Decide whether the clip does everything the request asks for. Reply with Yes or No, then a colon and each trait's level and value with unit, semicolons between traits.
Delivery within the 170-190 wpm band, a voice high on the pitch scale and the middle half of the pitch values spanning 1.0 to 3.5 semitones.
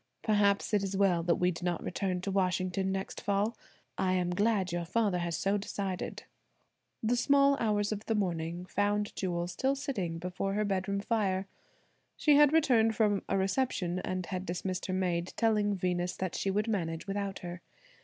Yes: average, 180 wpm; high, 195 Hz; narrow, 2.6 semitones